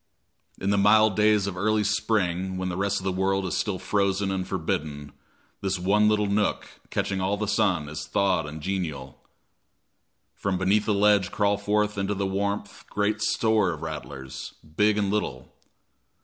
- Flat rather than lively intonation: Yes, narrow, 2.2 semitones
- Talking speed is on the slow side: No, average, 170 wpm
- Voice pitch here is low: Yes, low, 100 Hz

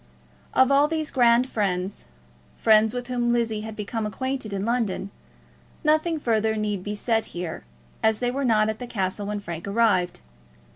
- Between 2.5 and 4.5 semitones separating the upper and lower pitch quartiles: Yes, average, 3.3 semitones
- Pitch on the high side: Yes, high, 220 Hz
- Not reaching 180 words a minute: Yes, average, 165 wpm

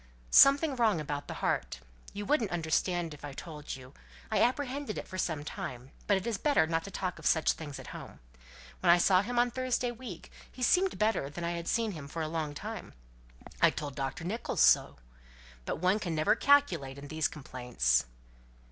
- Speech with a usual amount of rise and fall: No, wide, 7.5 semitones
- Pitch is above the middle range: No, medium, 170 Hz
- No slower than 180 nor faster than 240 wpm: Yes, average, 190 wpm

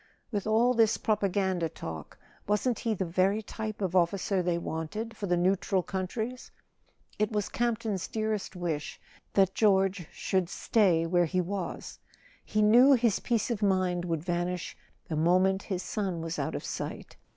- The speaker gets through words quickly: No, average, 160 wpm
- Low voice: No, high, 190 Hz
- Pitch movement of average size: Yes, average, 3.3 semitones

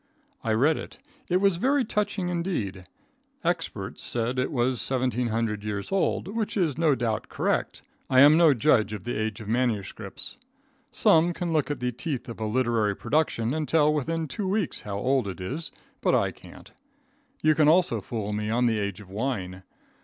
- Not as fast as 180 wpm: No, average, 185 wpm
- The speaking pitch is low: Yes, low, 130 Hz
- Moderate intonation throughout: No, wide, 6.8 semitones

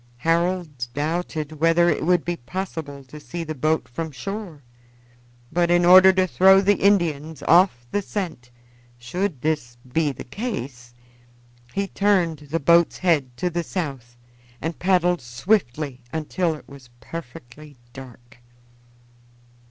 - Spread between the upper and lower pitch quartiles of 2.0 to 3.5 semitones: No, average, 4.4 semitones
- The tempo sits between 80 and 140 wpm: Yes, slow, 135 wpm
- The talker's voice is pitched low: No, medium, 160 Hz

